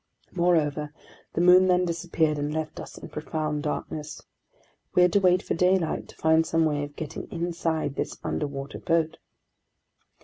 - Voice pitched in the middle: Yes, medium, 160 Hz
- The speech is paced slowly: No, average, 160 wpm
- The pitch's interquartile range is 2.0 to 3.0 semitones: Yes, narrow, 2.6 semitones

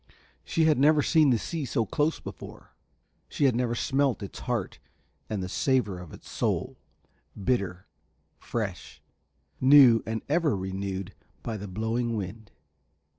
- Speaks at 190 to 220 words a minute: No, average, 140 wpm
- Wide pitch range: Yes, wide, 5.8 semitones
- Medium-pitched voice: No, low, 115 Hz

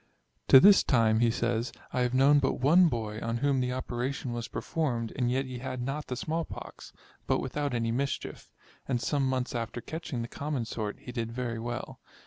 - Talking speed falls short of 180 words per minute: No, average, 200 wpm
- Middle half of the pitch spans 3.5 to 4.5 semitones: No, average, 2.8 semitones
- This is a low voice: Yes, low, 125 Hz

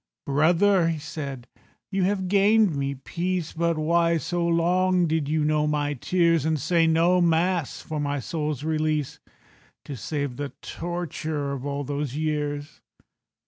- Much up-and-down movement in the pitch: No, average, 2.9 semitones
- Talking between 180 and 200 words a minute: No, average, 145 wpm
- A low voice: No, medium, 155 Hz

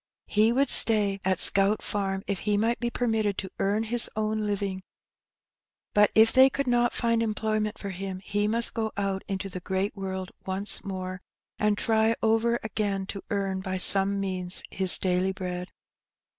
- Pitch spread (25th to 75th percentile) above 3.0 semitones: No, narrow, 2.4 semitones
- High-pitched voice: Yes, high, 200 Hz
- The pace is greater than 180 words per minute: No, average, 170 wpm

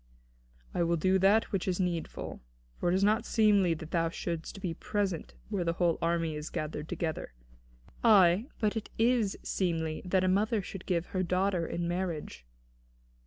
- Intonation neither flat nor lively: Yes, average, 3.0 semitones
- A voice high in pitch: No, medium, 180 Hz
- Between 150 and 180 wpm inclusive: Yes, average, 170 wpm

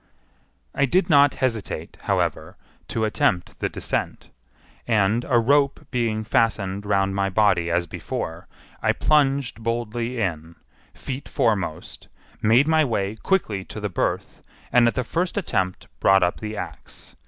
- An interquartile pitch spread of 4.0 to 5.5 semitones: Yes, average, 4.7 semitones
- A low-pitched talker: Yes, low, 110 Hz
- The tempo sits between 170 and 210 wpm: No, average, 140 wpm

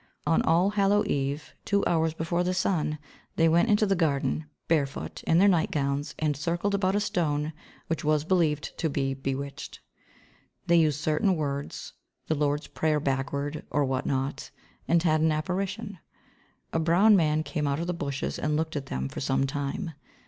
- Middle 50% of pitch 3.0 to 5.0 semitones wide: Yes, average, 3.4 semitones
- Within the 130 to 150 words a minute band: No, average, 175 wpm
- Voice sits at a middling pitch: Yes, medium, 155 Hz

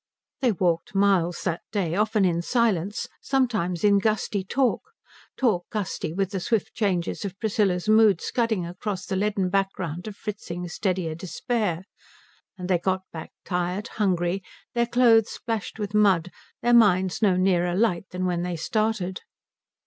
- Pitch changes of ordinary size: Yes, average, 3.3 semitones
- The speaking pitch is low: No, high, 195 Hz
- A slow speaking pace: No, average, 150 wpm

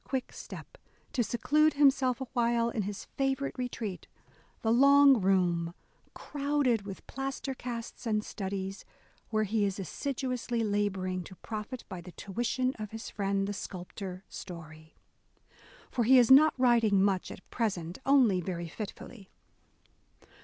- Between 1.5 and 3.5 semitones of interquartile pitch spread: No, average, 5.0 semitones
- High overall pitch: Yes, high, 220 Hz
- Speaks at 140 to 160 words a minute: Yes, average, 145 wpm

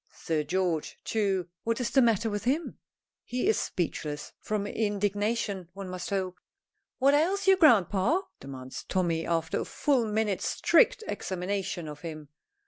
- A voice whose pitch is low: No, high, 200 Hz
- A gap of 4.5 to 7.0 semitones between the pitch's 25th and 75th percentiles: Yes, average, 4.8 semitones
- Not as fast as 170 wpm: Yes, average, 145 wpm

